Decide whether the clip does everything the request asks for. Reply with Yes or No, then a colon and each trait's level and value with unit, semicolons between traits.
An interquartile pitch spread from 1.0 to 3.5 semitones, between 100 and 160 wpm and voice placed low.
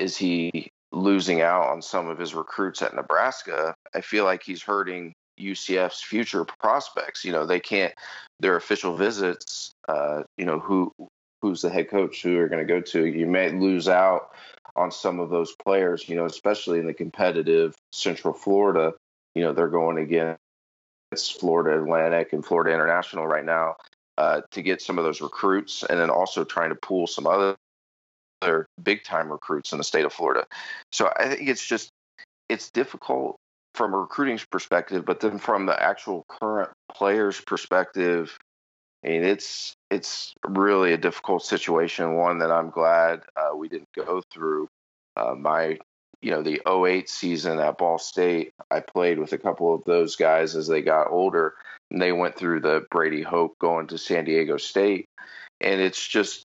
No: narrow, 2.5 semitones; average, 175 wpm; very low, 85 Hz